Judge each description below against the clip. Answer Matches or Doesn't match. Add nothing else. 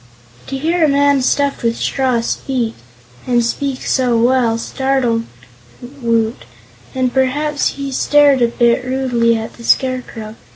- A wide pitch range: Doesn't match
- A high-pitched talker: Matches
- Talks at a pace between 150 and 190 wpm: Doesn't match